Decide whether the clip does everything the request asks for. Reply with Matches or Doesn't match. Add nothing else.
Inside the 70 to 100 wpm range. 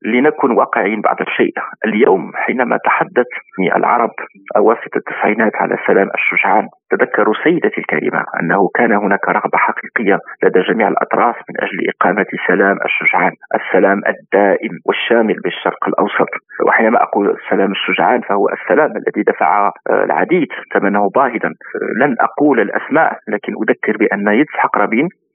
Doesn't match